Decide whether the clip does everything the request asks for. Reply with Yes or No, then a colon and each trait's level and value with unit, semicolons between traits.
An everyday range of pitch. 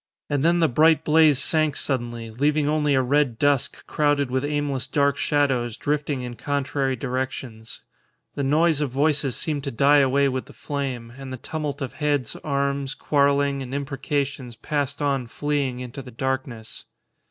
No: narrow, 2.1 semitones